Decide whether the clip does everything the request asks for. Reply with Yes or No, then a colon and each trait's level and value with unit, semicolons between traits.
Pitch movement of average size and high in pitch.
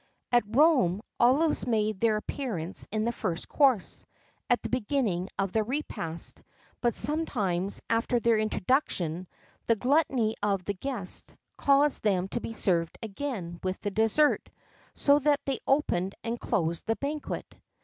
No: wide, 6.1 semitones; high, 225 Hz